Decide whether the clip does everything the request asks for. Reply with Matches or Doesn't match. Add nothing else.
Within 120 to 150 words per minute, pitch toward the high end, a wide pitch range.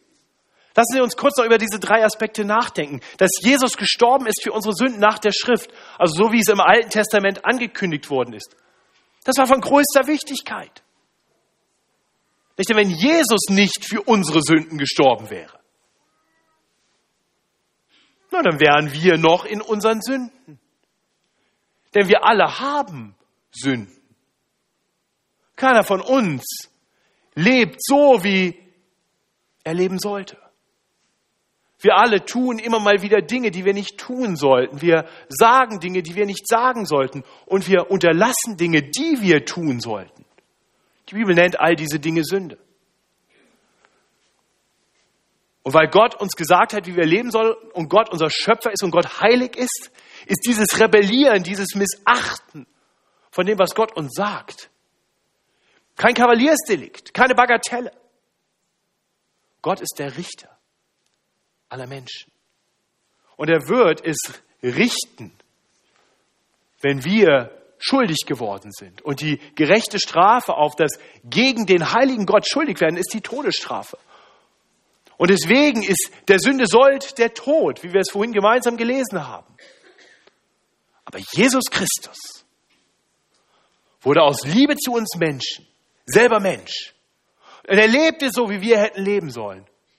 Matches